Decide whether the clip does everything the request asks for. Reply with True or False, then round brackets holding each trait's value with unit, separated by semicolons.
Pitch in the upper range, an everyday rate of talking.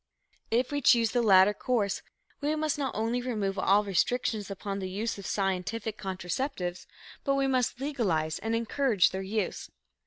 True (220 Hz; 160 wpm)